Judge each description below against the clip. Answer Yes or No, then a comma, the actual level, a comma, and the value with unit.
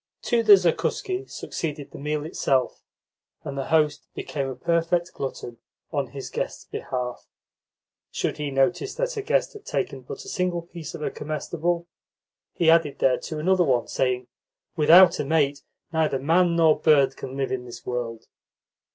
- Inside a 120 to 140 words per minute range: No, average, 160 wpm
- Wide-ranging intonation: No, average, 4.4 semitones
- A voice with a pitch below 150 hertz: No, medium, 155 Hz